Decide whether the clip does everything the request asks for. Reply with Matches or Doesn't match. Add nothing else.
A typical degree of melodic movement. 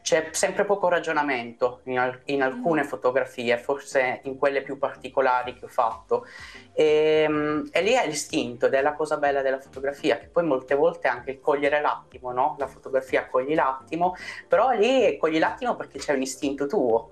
Matches